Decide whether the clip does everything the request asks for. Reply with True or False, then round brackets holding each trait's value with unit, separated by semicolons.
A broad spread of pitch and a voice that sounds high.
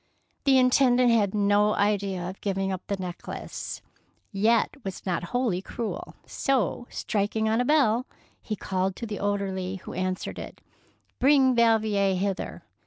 False (3.6 semitones; 205 Hz)